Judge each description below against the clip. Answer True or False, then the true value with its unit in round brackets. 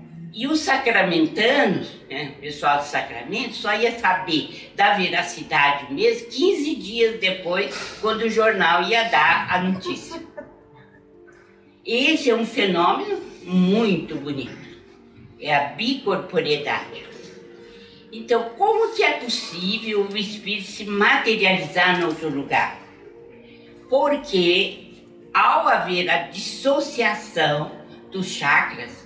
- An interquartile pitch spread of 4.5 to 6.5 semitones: True (5.3 semitones)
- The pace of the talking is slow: True (105 wpm)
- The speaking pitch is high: True (210 Hz)